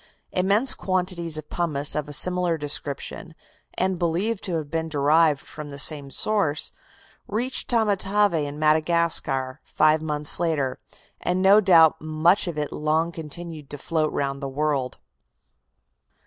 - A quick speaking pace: No, average, 140 wpm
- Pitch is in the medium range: Yes, medium, 160 Hz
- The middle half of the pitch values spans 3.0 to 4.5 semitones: Yes, average, 3.4 semitones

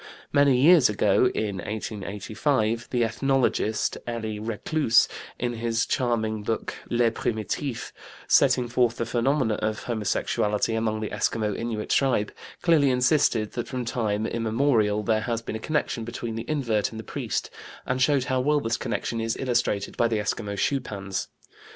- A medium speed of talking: Yes, average, 150 wpm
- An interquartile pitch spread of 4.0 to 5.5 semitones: No, average, 2.7 semitones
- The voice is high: No, low, 115 Hz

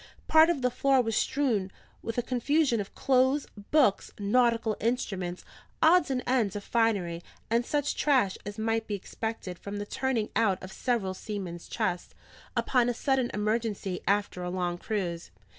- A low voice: No, high, 225 Hz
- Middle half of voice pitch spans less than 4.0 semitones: No, average, 4.3 semitones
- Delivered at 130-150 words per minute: No, average, 165 wpm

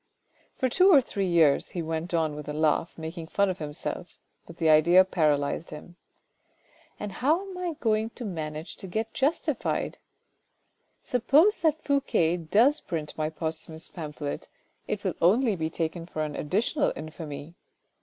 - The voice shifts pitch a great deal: Yes, wide, 6.1 semitones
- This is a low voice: No, medium, 170 Hz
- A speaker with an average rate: Yes, average, 165 wpm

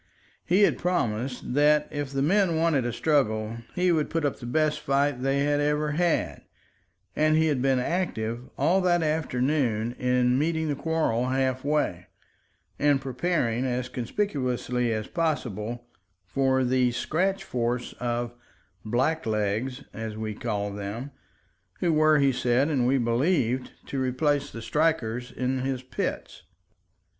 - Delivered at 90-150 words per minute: Yes, average, 140 wpm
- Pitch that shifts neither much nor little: Yes, average, 4.1 semitones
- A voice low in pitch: Yes, low, 130 Hz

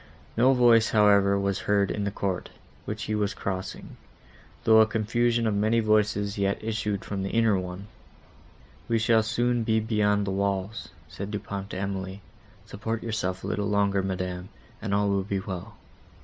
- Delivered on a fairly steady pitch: Yes, narrow, 2.1 semitones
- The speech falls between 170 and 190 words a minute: Yes, average, 175 wpm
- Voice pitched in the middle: No, low, 105 Hz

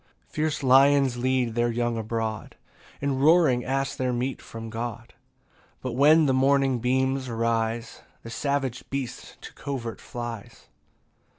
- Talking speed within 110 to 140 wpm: Yes, slow, 135 wpm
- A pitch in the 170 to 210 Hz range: No, low, 125 Hz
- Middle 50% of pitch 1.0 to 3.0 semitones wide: Yes, average, 2.7 semitones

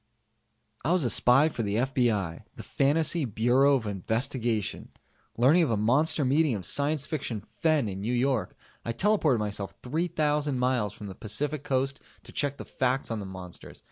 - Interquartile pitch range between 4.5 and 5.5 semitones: Yes, average, 5.0 semitones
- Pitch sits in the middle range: No, low, 130 Hz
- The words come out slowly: No, average, 170 wpm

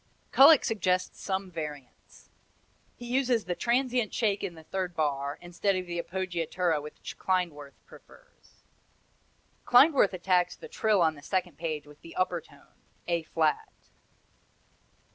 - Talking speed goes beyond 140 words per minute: No, slow, 135 wpm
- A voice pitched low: No, medium, 180 Hz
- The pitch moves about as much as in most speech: Yes, average, 3.9 semitones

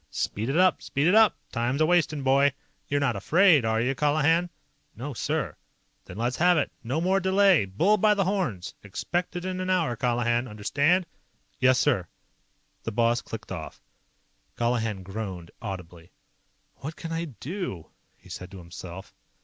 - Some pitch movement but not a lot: No, wide, 8.1 semitones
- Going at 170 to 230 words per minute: No, average, 160 wpm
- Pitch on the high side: No, low, 135 Hz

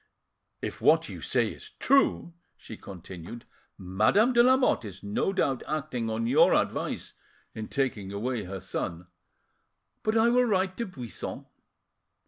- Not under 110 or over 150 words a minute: Yes, average, 140 wpm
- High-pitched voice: No, low, 120 Hz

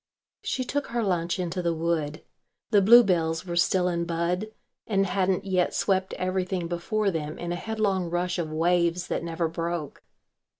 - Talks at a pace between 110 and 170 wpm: Yes, average, 165 wpm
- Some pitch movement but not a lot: No, narrow, 2.2 semitones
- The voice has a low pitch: No, medium, 175 Hz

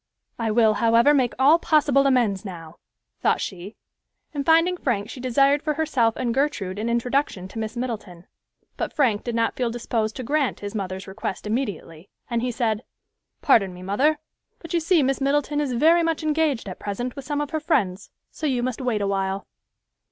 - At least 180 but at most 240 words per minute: Yes, average, 190 wpm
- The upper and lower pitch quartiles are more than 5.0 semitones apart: Yes, wide, 5.6 semitones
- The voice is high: Yes, high, 240 Hz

